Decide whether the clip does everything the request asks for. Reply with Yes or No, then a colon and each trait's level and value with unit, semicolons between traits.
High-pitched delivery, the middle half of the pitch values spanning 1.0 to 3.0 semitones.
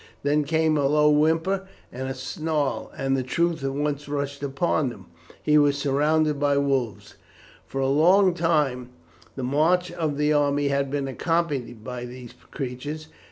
No: medium, 145 Hz; narrow, 2.5 semitones